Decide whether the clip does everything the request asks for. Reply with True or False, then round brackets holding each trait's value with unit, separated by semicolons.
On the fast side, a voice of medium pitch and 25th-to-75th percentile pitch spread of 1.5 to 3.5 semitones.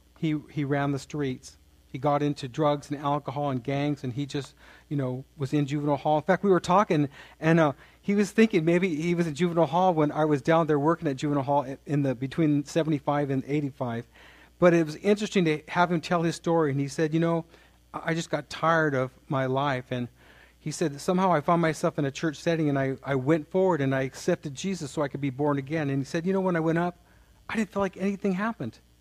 True (240 wpm; 150 Hz; 3.2 semitones)